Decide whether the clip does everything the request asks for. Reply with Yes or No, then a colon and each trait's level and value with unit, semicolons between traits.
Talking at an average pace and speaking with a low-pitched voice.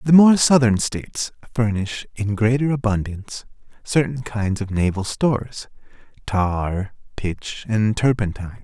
No: slow, 110 wpm; low, 115 Hz